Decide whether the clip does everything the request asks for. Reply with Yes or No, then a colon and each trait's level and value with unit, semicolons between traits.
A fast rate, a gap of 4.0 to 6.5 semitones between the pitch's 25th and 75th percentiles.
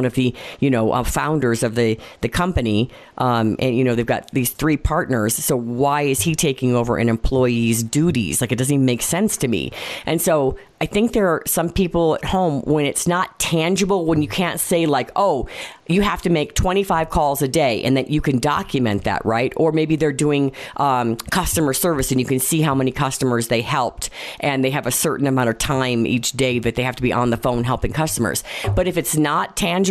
Yes: fast, 225 wpm; average, 4.6 semitones